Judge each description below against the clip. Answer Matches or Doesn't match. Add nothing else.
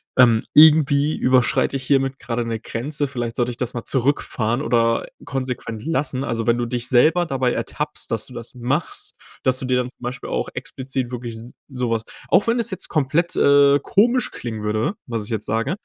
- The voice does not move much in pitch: Doesn't match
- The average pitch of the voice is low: Matches